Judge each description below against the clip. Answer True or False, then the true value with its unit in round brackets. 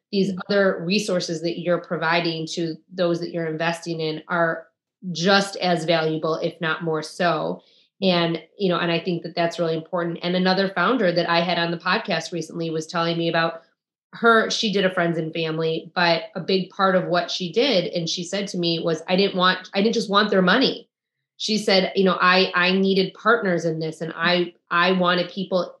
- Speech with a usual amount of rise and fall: False (2.2 semitones)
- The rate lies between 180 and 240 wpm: True (205 wpm)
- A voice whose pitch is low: False (175 Hz)